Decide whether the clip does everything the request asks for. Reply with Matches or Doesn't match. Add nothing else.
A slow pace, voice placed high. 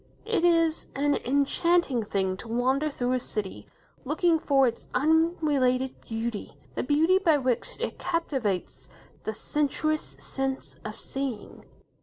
Matches